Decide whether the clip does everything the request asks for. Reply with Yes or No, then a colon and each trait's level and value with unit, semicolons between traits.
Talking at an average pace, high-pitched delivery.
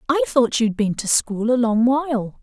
No: fast, 220 wpm; high, 235 Hz